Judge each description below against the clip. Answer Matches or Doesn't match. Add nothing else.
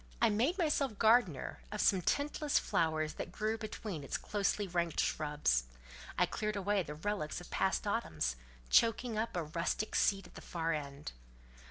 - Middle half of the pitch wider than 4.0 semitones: Matches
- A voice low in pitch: Doesn't match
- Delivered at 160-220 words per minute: Matches